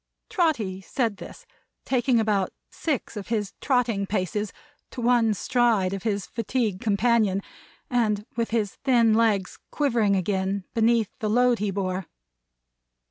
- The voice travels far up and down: No, average, 3.2 semitones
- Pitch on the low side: No, high, 220 Hz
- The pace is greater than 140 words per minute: No, slow, 135 wpm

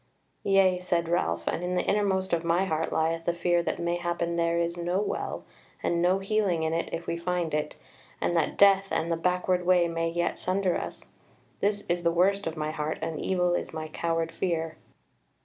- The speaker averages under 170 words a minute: No, average, 200 wpm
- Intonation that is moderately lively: No, narrow, 1.6 semitones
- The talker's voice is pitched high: No, medium, 170 Hz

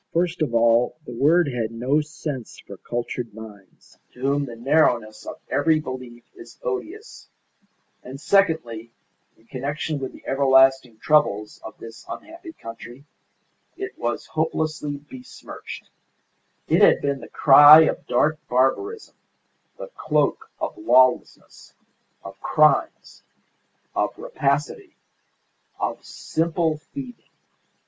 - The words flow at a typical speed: No, slow, 120 wpm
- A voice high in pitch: No, medium, 140 Hz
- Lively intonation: No, average, 4.8 semitones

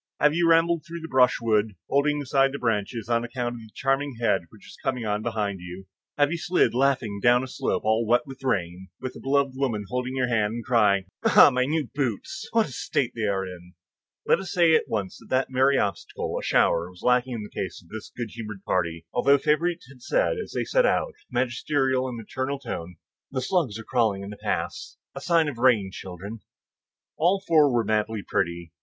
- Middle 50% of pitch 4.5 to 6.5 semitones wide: Yes, average, 4.9 semitones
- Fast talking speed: Yes, fast, 215 wpm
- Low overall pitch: Yes, low, 125 Hz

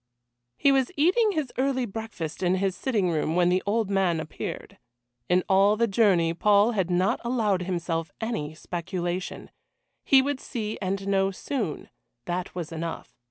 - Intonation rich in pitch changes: No, average, 4.6 semitones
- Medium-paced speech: Yes, average, 160 wpm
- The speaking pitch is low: No, high, 195 Hz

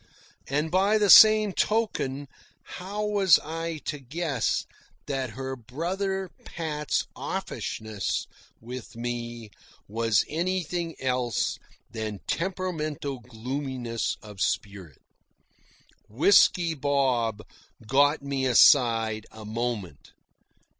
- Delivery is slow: Yes, slow, 90 wpm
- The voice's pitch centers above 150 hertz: No, low, 135 Hz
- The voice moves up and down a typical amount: No, wide, 6.4 semitones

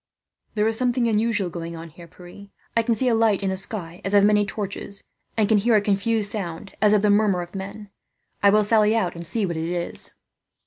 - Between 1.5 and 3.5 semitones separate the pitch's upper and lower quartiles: Yes, average, 3.2 semitones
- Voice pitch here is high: Yes, high, 205 Hz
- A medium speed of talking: No, fast, 225 wpm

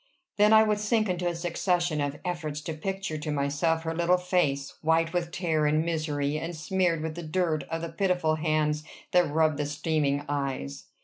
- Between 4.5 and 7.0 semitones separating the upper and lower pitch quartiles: No, average, 2.7 semitones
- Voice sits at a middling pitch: Yes, medium, 160 Hz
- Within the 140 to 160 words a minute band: No, average, 190 wpm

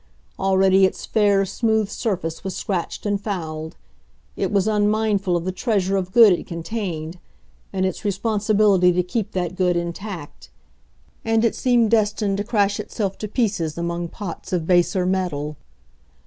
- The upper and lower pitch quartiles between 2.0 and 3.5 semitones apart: Yes, average, 2.9 semitones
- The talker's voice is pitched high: Yes, high, 195 Hz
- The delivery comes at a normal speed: Yes, average, 150 wpm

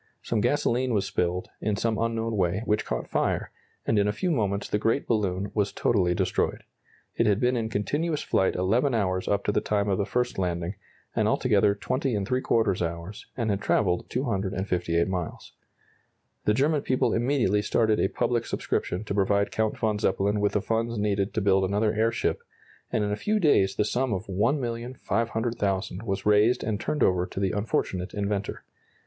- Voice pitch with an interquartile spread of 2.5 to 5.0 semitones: Yes, average, 3.0 semitones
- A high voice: No, low, 105 Hz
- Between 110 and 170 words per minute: No, average, 180 wpm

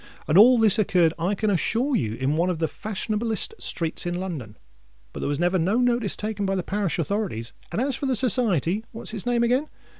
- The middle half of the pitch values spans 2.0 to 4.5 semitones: No, wide, 5.4 semitones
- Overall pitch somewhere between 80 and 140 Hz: No, high, 200 Hz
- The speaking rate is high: Yes, fast, 215 wpm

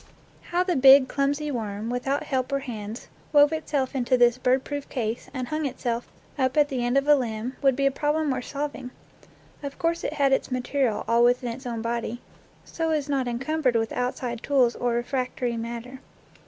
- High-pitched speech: Yes, very high, 260 Hz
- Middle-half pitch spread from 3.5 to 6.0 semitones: No, average, 3.0 semitones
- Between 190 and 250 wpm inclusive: Yes, average, 195 wpm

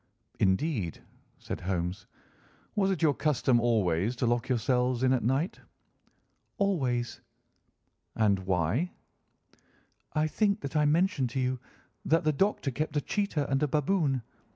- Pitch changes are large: No, average, 4.8 semitones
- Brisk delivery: No, slow, 135 wpm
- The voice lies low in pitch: Yes, low, 130 Hz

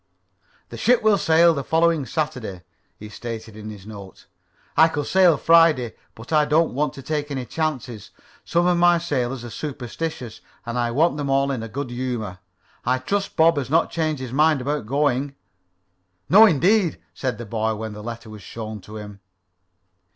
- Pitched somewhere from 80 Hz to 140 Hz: Yes, low, 135 Hz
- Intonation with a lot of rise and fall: Yes, wide, 5.8 semitones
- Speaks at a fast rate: No, average, 185 wpm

